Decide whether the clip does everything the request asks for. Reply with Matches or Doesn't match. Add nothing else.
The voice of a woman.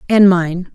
Matches